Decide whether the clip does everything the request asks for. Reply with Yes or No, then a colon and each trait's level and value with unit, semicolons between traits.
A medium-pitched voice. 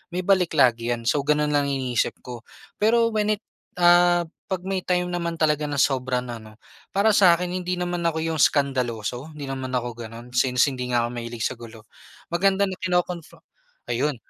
Yes: medium, 150 Hz